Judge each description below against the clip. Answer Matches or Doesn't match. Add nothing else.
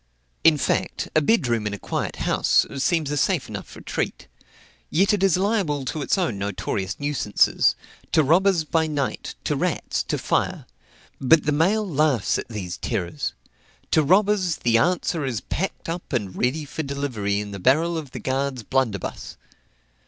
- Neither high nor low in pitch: Matches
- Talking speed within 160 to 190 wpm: Matches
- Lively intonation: Matches